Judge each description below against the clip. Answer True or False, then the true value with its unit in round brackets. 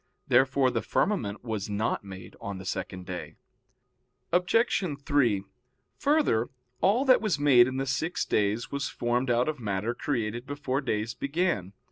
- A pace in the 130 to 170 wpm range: True (150 wpm)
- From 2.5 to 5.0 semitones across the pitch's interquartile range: False (5.5 semitones)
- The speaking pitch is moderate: False (125 Hz)